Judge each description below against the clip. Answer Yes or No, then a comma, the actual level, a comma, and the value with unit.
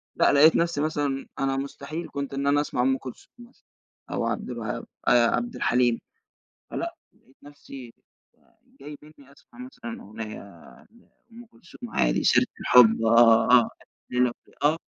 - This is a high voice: No, medium, 140 Hz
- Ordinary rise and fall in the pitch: Yes, average, 4.0 semitones